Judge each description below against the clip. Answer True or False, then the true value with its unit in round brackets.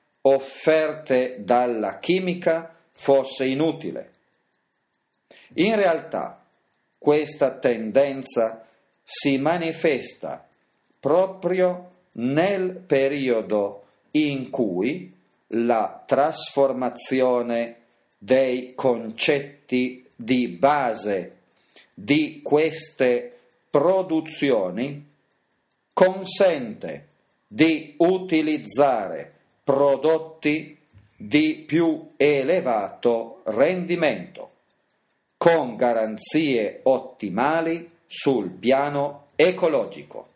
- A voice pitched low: False (145 Hz)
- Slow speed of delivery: True (60 wpm)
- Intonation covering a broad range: False (4.7 semitones)